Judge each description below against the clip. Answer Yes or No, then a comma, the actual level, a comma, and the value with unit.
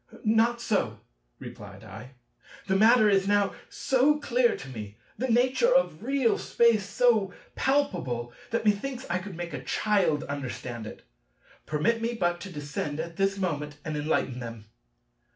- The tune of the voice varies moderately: No, wide, 8.2 semitones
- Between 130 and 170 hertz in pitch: No, high, 195 Hz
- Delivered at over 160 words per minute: No, average, 150 wpm